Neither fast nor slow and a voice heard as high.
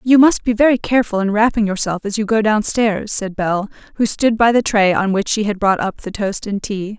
No: fast, 250 wpm; high, 210 Hz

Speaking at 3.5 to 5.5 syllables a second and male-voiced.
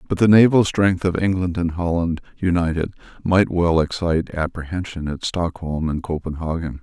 Yes: 5.0 syllables/s; male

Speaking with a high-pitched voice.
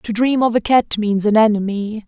Yes: high, 220 Hz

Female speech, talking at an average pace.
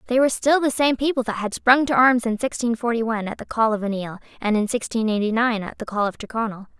No: female; fast, 265 wpm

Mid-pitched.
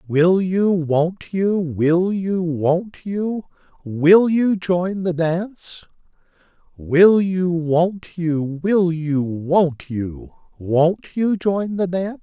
Yes: medium, 175 Hz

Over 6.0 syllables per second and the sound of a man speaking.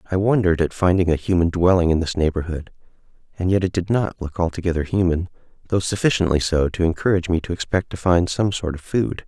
Yes: 6.3 syllables/s; male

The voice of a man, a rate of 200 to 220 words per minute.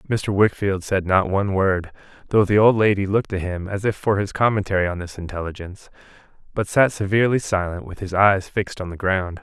Yes: male; fast, 205 wpm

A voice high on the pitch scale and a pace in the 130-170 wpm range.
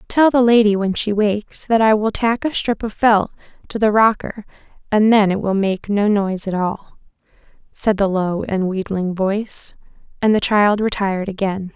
No: high, 205 Hz; average, 190 wpm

